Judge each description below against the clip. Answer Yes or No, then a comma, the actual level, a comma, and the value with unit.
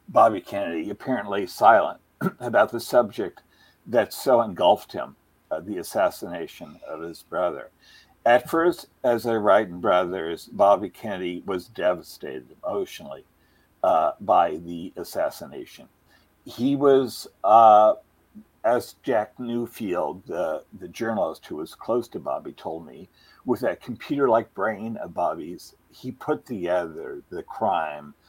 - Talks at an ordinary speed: No, slow, 130 wpm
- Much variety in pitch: Yes, wide, 6.0 semitones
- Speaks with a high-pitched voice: No, low, 110 Hz